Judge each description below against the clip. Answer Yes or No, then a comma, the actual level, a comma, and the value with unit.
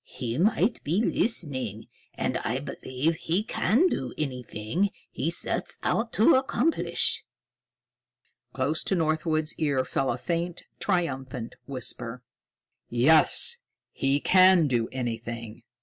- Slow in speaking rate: Yes, slow, 115 wpm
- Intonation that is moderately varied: No, wide, 6.5 semitones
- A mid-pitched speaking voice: Yes, medium, 155 Hz